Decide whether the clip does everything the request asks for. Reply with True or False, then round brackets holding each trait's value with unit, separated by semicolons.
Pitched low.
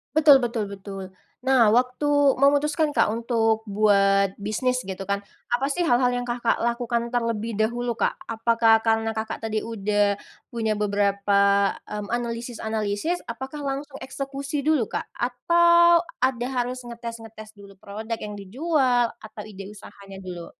False (230 Hz)